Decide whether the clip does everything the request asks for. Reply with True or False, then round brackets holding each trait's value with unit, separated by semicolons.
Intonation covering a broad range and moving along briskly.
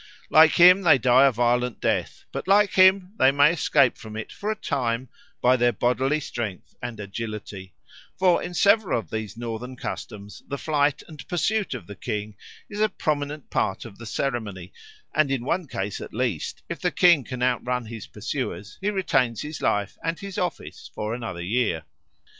False (6.2 semitones; 180 wpm)